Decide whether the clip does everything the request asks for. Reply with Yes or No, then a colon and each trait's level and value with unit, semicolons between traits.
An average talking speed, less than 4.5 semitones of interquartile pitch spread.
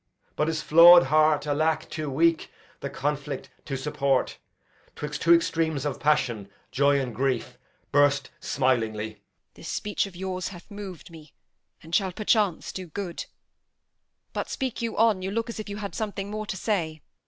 No: average, 165 wpm; average, 5.1 semitones